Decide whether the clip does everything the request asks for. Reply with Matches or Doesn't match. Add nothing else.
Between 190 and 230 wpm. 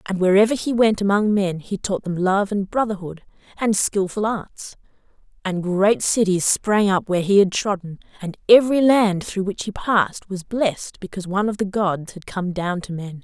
Matches